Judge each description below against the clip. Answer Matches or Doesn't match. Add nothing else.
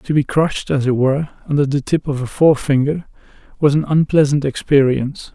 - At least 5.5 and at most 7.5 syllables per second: Matches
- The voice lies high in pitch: Doesn't match